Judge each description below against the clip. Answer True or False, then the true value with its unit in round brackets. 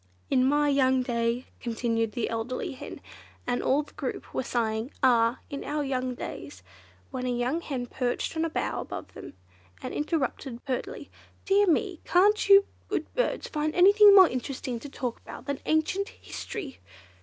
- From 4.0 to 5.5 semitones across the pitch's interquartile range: True (4.6 semitones)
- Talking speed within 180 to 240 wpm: False (165 wpm)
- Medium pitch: False (265 Hz)